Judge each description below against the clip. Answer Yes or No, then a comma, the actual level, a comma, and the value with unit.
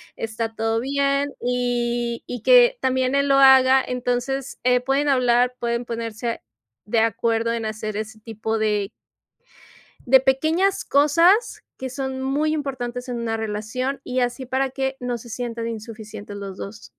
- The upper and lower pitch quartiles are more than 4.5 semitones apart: No, average, 2.9 semitones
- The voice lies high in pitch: Yes, high, 245 Hz